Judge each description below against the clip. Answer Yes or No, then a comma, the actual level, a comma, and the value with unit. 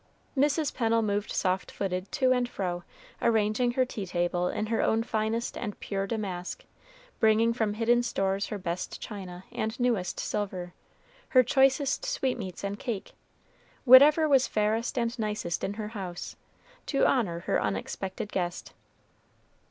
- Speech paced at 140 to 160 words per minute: Yes, average, 145 wpm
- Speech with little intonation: No, average, 4.2 semitones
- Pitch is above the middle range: Yes, high, 215 Hz